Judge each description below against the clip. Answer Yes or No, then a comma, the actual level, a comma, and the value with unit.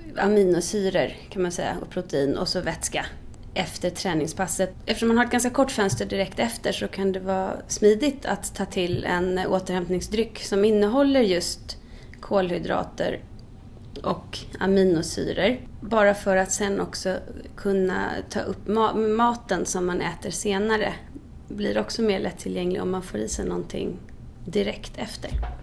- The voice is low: No, high, 190 Hz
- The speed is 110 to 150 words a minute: Yes, average, 145 wpm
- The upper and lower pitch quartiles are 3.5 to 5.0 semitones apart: No, narrow, 2.5 semitones